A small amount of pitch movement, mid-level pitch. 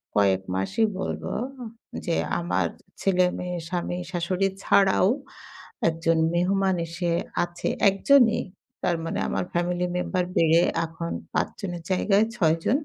Yes: narrow, 2.3 semitones; medium, 175 Hz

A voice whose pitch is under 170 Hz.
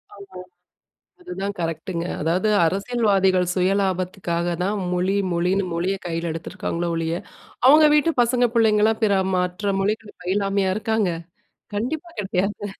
No: high, 195 Hz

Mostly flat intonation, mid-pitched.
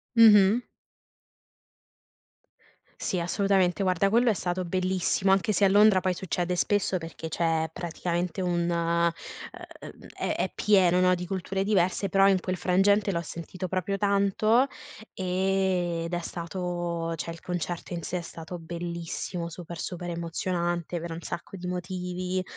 Yes: narrow, 2.0 semitones; medium, 180 Hz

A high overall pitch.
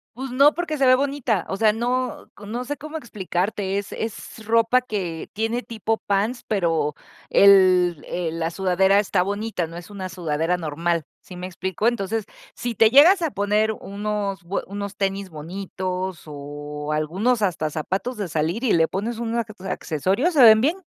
Yes: high, 200 Hz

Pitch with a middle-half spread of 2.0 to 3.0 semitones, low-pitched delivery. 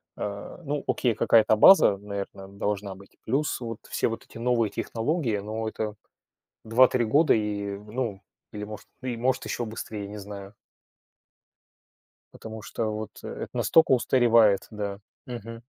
Yes: narrow, 2.6 semitones; low, 110 Hz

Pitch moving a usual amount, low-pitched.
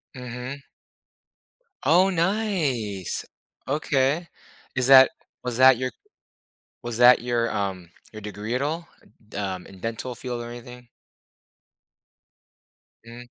Yes: average, 3.2 semitones; low, 125 Hz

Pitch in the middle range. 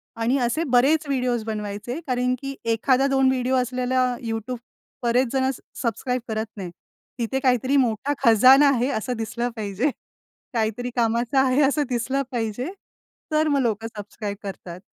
No: high, 245 Hz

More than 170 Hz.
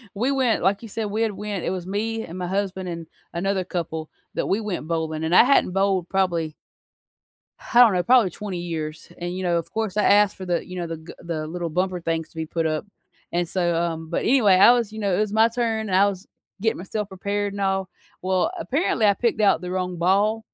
Yes: high, 190 Hz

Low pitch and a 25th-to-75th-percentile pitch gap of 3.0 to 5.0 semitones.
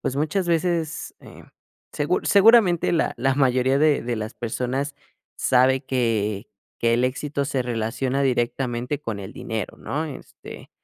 Yes: low, 130 Hz; average, 3.6 semitones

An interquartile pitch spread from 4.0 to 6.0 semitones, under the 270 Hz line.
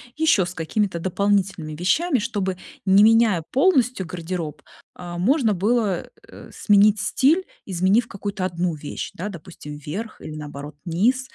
Yes: average, 4.7 semitones; high, 190 Hz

